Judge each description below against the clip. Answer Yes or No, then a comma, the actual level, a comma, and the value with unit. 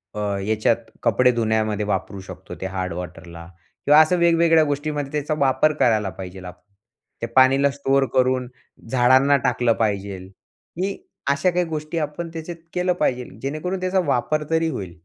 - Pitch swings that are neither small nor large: No, wide, 6.6 semitones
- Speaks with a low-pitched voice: Yes, low, 130 Hz